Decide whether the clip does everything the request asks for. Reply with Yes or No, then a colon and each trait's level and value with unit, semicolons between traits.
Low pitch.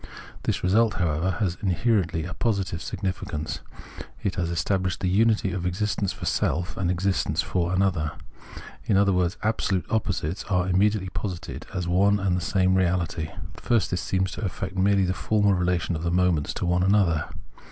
Yes: very low, 95 Hz